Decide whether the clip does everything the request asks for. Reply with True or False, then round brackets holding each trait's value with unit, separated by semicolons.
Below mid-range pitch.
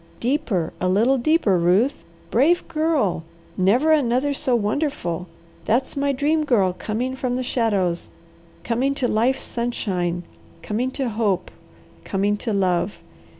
False (235 Hz)